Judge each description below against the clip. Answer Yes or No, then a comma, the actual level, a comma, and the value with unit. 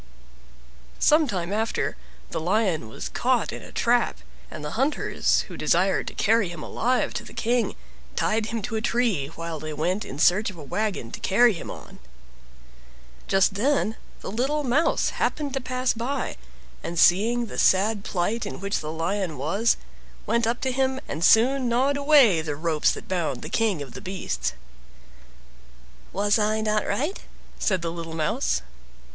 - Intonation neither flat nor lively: No, wide, 6.2 semitones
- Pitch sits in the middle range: No, high, 210 Hz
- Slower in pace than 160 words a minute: No, average, 170 wpm